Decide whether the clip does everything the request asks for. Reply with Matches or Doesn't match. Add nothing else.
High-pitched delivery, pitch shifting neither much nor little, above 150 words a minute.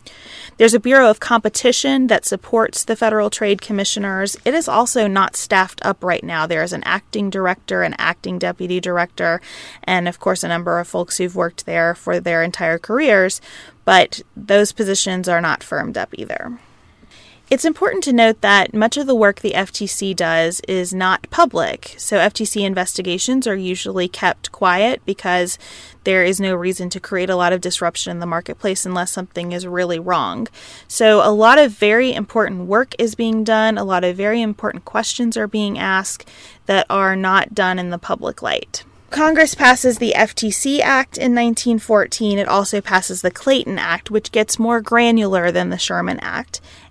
Matches